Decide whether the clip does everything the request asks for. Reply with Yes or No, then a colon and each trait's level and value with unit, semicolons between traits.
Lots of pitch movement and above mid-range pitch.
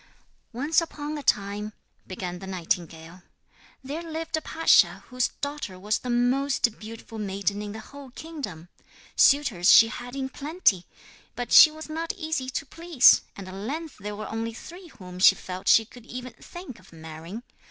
Yes: wide, 7.0 semitones; high, 240 Hz